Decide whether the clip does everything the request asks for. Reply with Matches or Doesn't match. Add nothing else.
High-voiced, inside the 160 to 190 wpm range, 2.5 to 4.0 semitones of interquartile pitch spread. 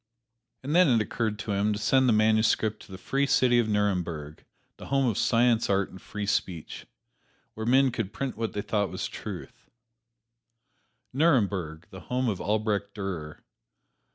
Doesn't match